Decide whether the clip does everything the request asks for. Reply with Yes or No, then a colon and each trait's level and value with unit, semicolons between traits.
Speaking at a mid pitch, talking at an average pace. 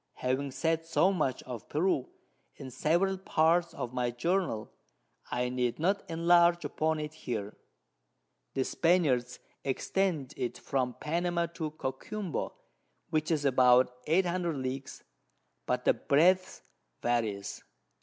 No: medium, 150 Hz; slow, 120 wpm